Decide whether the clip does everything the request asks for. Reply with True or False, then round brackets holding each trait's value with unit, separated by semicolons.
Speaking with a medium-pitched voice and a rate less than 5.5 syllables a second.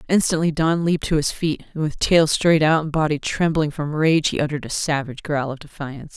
False (155 Hz; 5.8 syllables/s)